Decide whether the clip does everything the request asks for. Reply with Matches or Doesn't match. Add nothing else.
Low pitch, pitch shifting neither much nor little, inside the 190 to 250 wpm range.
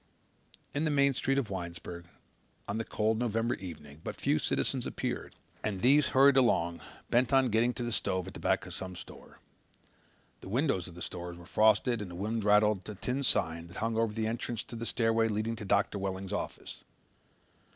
Matches